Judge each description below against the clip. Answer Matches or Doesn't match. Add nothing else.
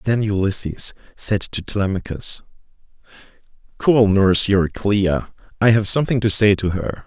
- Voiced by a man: Matches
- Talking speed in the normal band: Doesn't match